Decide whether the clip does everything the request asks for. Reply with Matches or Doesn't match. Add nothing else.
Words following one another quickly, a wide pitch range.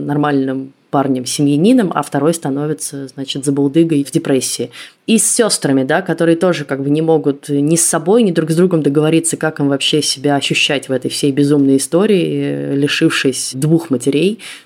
Doesn't match